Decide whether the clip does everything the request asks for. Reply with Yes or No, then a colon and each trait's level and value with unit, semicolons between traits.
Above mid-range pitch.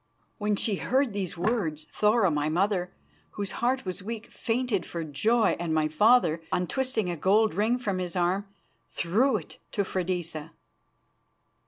Yes: high, 195 Hz